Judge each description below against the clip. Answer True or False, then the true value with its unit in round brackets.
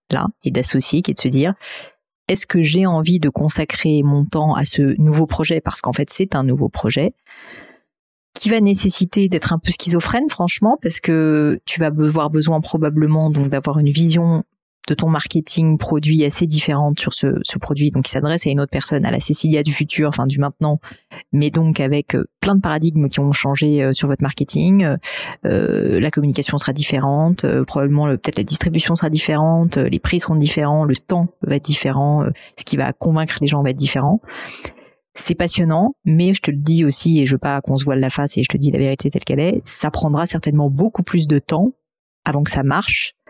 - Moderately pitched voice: True (155 Hz)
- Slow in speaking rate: False (215 wpm)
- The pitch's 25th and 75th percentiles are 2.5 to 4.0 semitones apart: True (2.9 semitones)